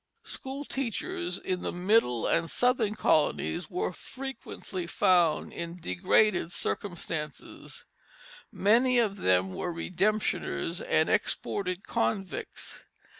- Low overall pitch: No, medium, 185 Hz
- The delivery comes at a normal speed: No, slow, 100 wpm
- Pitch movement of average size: Yes, average, 4.6 semitones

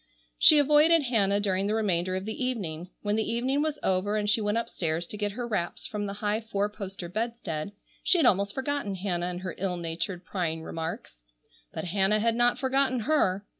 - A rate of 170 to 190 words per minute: No, average, 200 wpm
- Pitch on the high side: Yes, high, 205 Hz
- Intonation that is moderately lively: Yes, average, 4.1 semitones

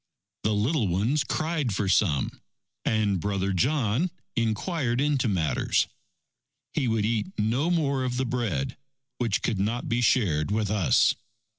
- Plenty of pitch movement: No, average, 4.5 semitones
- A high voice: No, low, 115 Hz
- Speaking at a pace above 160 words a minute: No, average, 140 wpm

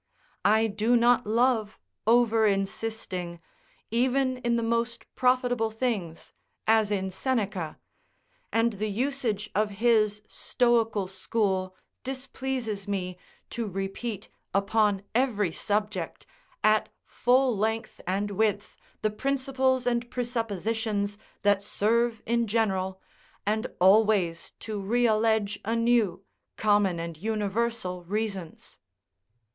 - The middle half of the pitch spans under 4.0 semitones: Yes, average, 2.9 semitones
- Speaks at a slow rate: Yes, slow, 105 wpm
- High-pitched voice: Yes, high, 220 Hz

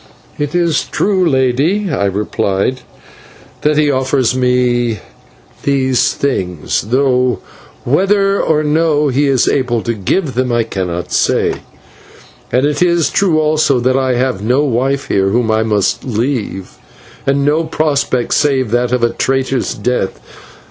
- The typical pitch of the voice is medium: No, low, 130 Hz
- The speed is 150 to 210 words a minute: No, average, 140 wpm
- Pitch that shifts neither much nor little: Yes, average, 3.8 semitones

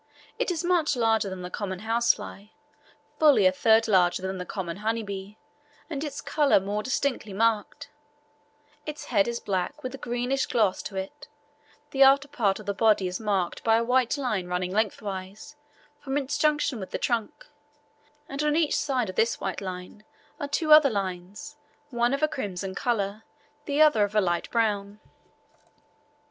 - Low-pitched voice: No, high, 220 Hz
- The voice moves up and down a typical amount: No, wide, 5.8 semitones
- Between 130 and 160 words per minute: No, average, 175 wpm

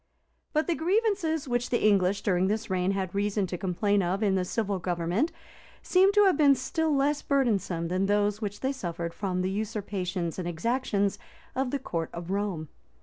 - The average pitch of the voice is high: Yes, high, 205 Hz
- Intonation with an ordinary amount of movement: No, wide, 6.3 semitones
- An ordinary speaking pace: Yes, average, 190 wpm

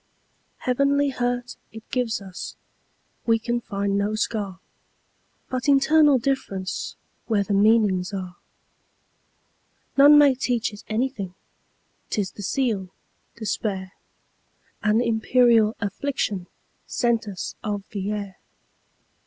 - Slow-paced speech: Yes, slow, 85 wpm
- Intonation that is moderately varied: Yes, average, 3.8 semitones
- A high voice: Yes, high, 220 Hz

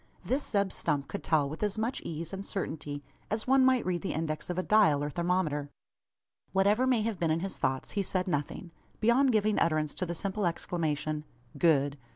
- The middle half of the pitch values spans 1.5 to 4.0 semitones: No, wide, 5.4 semitones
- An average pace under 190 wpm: No, average, 195 wpm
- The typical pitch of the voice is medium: Yes, medium, 180 Hz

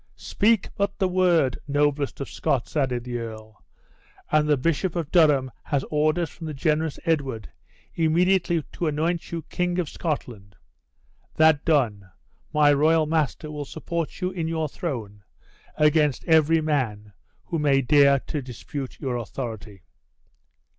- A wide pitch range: No, average, 3.8 semitones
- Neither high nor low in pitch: Yes, medium, 150 Hz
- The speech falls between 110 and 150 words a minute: Yes, average, 140 wpm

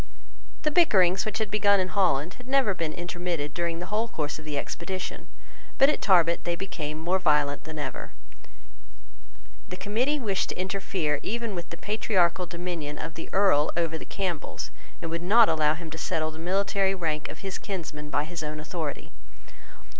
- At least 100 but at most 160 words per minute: No, average, 180 wpm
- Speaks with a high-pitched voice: No, medium, 175 Hz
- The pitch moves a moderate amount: Yes, average, 3.8 semitones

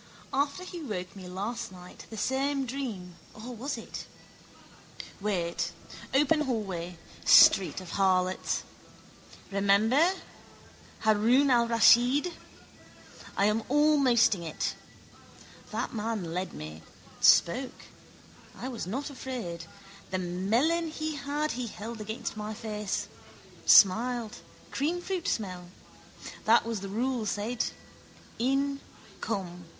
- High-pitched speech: Yes, high, 225 Hz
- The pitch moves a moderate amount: No, wide, 5.7 semitones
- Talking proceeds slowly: Yes, slow, 105 wpm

